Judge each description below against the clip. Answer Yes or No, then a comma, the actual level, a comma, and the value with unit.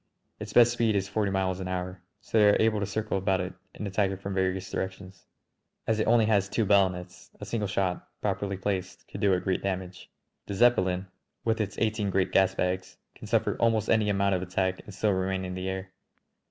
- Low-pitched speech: Yes, very low, 95 Hz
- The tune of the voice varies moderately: No, narrow, 2.1 semitones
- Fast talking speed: Yes, fast, 210 wpm